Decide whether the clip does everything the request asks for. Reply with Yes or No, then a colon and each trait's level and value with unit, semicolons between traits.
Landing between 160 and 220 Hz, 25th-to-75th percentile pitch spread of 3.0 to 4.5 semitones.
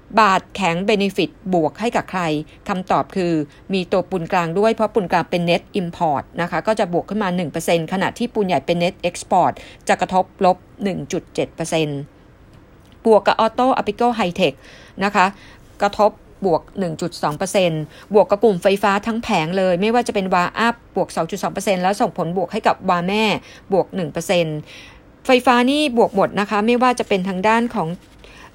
Yes: high, 190 Hz; average, 3.8 semitones